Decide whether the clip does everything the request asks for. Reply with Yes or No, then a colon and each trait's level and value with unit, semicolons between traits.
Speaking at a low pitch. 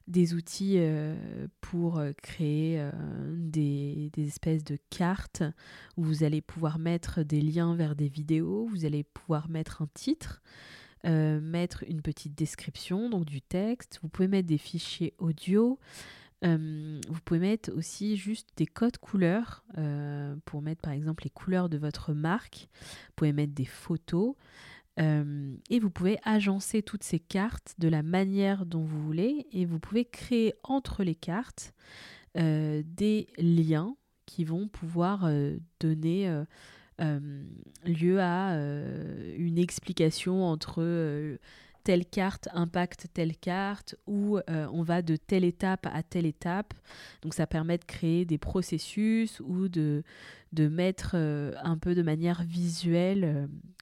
No: medium, 170 Hz